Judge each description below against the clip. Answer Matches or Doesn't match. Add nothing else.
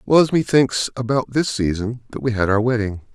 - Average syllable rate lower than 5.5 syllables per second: Matches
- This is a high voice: Doesn't match